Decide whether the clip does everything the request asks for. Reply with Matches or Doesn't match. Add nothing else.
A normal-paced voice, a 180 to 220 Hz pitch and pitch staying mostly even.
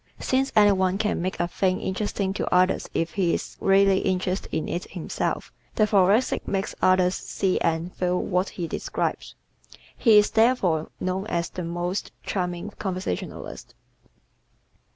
Matches